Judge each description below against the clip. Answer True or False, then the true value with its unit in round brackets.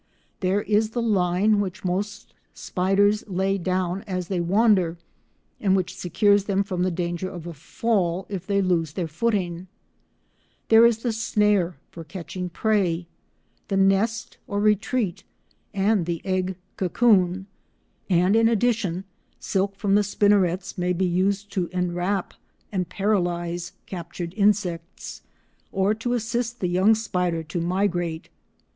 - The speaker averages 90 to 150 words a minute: True (140 wpm)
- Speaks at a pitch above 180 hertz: True (190 Hz)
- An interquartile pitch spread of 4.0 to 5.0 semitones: False (2.7 semitones)